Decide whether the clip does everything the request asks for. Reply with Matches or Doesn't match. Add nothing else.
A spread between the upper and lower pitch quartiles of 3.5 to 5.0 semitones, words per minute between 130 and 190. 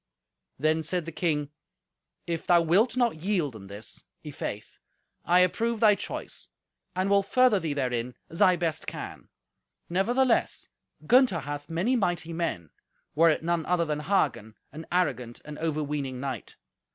Matches